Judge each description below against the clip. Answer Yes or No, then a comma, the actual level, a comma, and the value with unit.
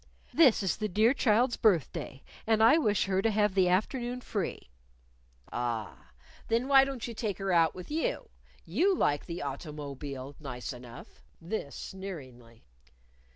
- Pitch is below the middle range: No, high, 190 Hz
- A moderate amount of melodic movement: No, wide, 8.0 semitones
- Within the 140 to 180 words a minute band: Yes, average, 155 wpm